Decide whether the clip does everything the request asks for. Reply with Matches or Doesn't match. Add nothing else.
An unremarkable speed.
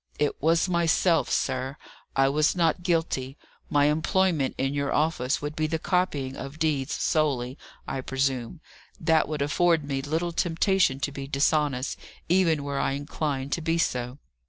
Matches